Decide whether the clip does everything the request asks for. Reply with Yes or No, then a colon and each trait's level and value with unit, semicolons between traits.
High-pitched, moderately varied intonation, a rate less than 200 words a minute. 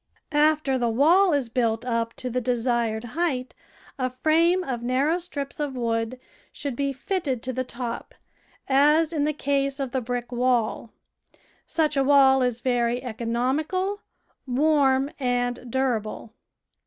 Yes: very high, 255 Hz; average, 3.1 semitones; average, 140 wpm